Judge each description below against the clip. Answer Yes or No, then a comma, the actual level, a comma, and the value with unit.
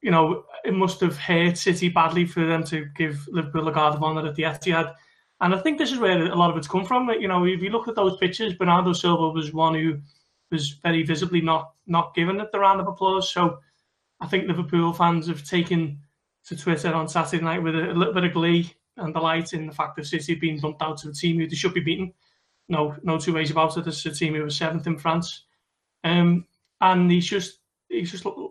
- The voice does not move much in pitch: Yes, narrow, 2.0 semitones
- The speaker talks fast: Yes, fast, 235 wpm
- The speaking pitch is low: No, medium, 170 Hz